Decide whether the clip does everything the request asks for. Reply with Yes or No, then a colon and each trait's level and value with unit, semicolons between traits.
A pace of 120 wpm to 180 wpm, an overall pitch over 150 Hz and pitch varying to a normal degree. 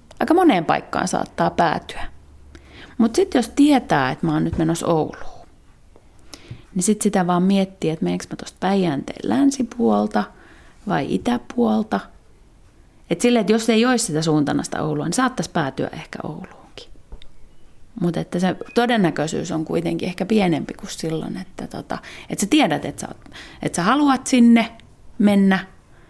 No: average, 150 wpm; medium, 185 Hz; wide, 7.4 semitones